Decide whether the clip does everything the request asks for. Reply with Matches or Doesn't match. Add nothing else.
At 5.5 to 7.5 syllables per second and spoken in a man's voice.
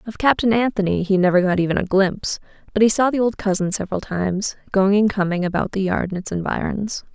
Doesn't match